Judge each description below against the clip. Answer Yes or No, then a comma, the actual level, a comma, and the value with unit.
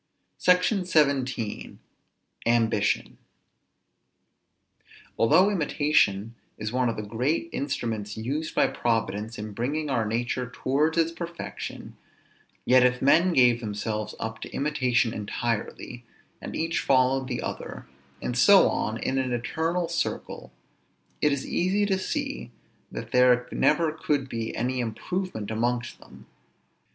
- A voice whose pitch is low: Yes, low, 125 Hz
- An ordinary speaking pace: No, slow, 125 wpm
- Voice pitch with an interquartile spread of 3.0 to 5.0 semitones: No, wide, 5.4 semitones